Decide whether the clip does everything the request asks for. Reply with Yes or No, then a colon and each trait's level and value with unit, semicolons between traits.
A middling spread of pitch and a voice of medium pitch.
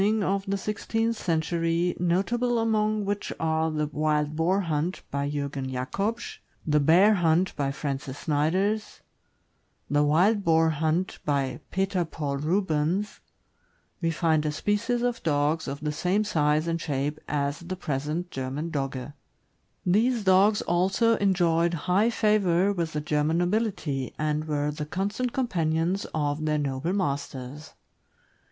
Yes: average, 4.9 semitones; medium, 165 Hz